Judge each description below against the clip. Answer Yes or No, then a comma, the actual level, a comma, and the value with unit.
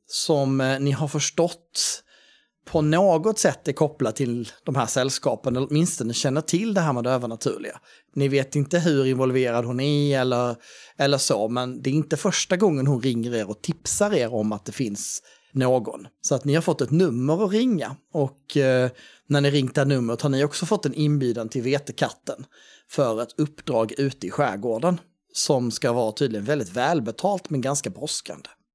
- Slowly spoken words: No, average, 185 wpm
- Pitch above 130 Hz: Yes, medium, 140 Hz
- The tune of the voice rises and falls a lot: No, average, 3.6 semitones